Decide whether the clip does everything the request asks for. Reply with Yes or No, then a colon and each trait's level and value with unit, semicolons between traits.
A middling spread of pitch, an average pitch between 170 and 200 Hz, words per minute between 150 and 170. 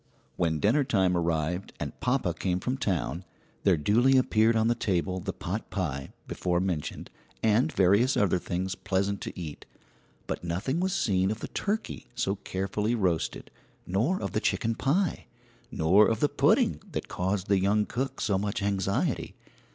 No: average, 4.3 semitones; low, 100 Hz; average, 160 wpm